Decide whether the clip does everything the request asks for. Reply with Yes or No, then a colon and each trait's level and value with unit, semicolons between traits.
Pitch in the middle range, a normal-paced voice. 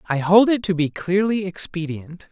Yes: medium, 180 Hz; average, 180 wpm